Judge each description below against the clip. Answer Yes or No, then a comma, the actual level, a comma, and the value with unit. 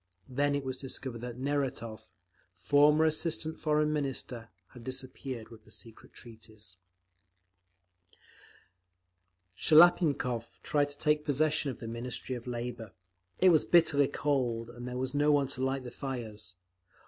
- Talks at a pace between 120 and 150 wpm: Yes, slow, 135 wpm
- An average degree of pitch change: Yes, average, 3.7 semitones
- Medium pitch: No, low, 130 Hz